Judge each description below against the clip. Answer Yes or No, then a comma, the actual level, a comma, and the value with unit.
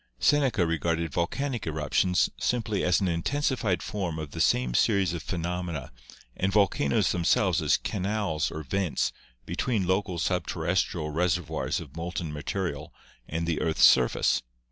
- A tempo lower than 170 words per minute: Yes, average, 145 wpm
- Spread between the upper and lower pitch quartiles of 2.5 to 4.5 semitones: Yes, average, 3.4 semitones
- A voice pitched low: Yes, very low, 85 Hz